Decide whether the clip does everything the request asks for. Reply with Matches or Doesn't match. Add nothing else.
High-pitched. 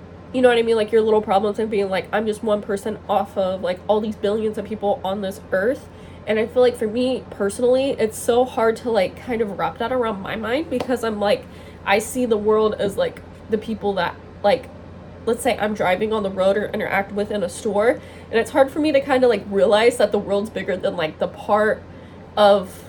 Matches